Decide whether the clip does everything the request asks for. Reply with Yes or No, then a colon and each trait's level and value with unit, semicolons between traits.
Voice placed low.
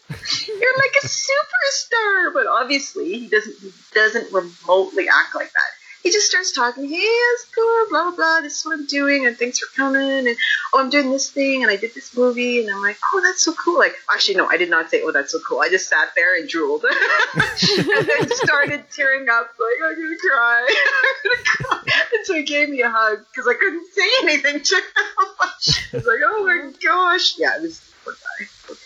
No: very high, 295 Hz